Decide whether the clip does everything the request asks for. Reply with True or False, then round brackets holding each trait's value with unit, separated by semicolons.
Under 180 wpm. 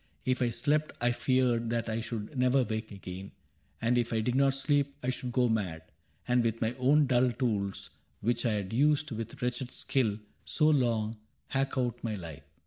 False (190 wpm)